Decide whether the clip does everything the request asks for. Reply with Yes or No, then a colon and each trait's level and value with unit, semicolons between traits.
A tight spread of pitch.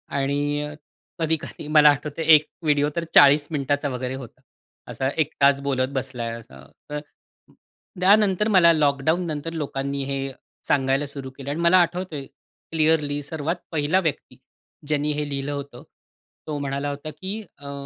Yes: narrow, 2.3 semitones